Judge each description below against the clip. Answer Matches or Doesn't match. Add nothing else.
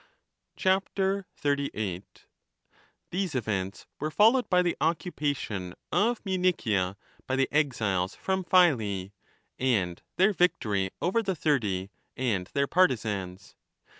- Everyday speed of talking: Doesn't match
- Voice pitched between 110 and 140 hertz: Matches